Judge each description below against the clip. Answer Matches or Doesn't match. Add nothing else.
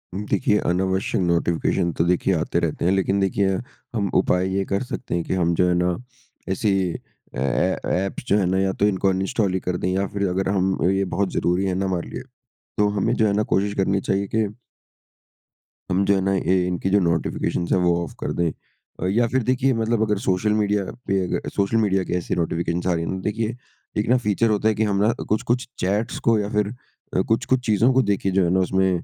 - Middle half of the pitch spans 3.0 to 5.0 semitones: Doesn't match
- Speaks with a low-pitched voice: Matches